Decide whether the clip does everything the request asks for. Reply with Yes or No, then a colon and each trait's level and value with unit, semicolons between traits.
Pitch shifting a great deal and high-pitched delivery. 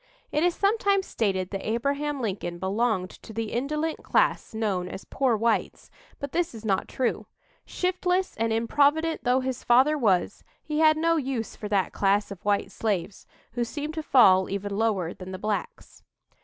Yes: wide, 6.9 semitones; high, 230 Hz